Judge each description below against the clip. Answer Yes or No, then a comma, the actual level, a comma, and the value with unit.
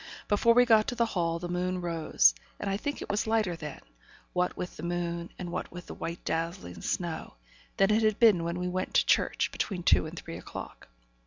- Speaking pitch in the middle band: Yes, medium, 180 Hz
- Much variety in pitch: No, average, 3.4 semitones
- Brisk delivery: Yes, fast, 220 wpm